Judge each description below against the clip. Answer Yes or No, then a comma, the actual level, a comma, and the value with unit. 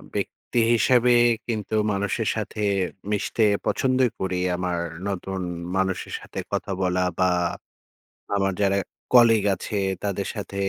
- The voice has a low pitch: Yes, low, 100 Hz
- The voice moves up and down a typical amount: Yes, average, 3.0 semitones